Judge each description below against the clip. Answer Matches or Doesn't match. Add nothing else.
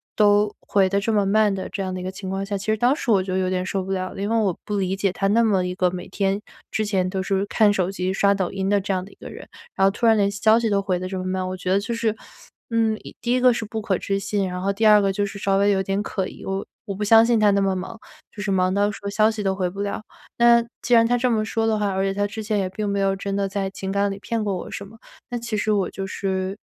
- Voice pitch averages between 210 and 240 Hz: Doesn't match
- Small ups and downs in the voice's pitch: Matches